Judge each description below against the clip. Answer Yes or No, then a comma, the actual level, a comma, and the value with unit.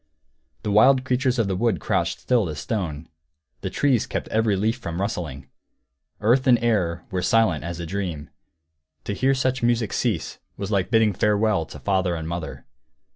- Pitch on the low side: Yes, low, 105 Hz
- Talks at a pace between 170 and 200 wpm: Yes, average, 175 wpm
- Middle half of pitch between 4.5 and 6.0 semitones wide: Yes, wide, 5.4 semitones